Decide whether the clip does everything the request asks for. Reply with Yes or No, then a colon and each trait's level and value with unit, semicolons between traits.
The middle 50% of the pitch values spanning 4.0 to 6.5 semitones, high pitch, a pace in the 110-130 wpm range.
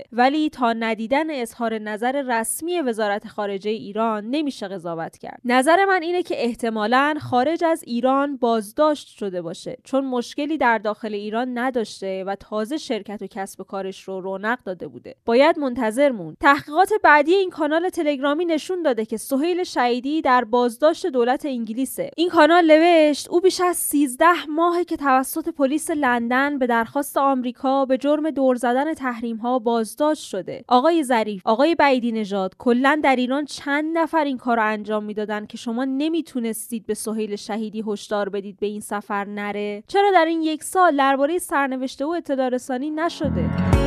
No: wide, 5.5 semitones; very high, 255 Hz; fast, 155 wpm